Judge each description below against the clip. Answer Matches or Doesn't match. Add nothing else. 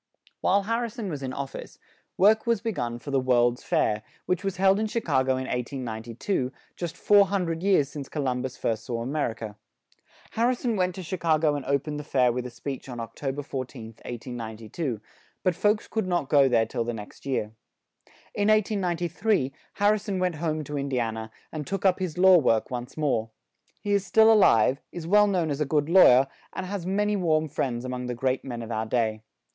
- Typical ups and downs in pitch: Doesn't match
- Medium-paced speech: Doesn't match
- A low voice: Doesn't match